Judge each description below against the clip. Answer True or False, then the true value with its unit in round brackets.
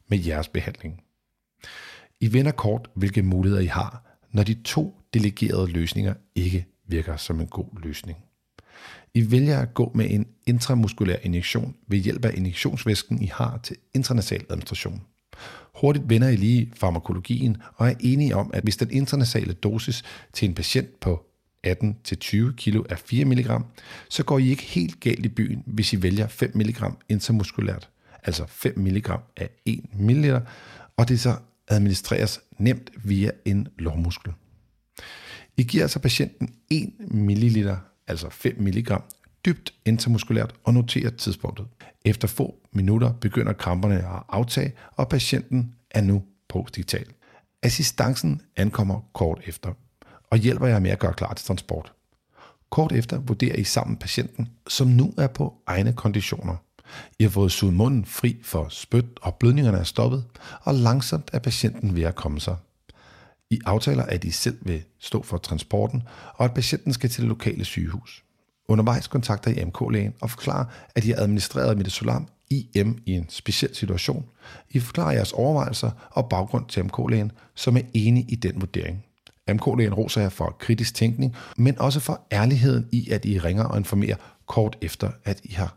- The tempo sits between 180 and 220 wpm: False (160 wpm)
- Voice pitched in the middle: False (110 Hz)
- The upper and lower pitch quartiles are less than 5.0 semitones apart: True (3.8 semitones)